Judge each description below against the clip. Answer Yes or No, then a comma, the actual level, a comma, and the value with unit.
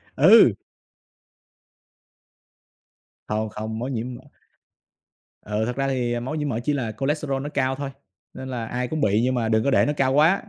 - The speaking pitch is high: No, low, 130 Hz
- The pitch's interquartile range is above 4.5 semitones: No, average, 3.5 semitones